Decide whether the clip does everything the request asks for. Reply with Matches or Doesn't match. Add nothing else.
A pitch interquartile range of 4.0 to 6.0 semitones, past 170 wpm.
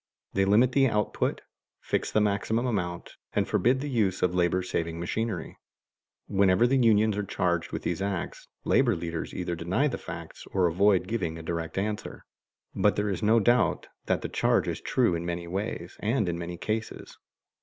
Matches